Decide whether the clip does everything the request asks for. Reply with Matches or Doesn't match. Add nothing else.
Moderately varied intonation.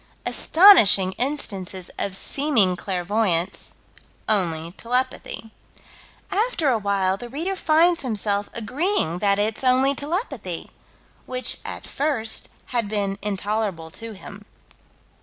Doesn't match